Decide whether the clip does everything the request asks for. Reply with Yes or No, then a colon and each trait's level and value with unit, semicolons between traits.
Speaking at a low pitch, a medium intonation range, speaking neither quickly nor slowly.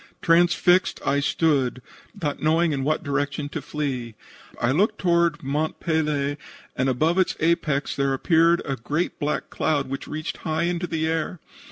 No: medium, 155 Hz; average, 3.0 semitones; average, 160 wpm